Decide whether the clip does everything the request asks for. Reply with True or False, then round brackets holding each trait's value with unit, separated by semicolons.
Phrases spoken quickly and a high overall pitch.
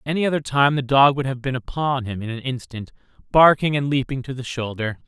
False (235 wpm; 130 Hz)